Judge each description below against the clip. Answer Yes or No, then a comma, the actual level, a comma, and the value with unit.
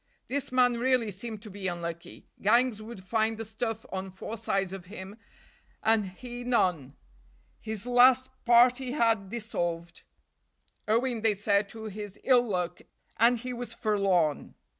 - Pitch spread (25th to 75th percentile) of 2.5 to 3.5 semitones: No, average, 4.0 semitones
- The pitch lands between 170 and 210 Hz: No, high, 220 Hz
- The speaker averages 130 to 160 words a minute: Yes, average, 145 wpm